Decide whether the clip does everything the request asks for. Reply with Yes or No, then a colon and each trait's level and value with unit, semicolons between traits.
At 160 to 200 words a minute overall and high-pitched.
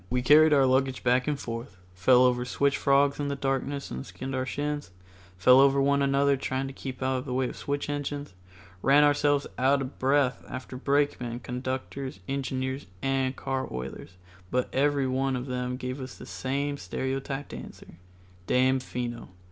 No: average, 165 wpm; low, 135 Hz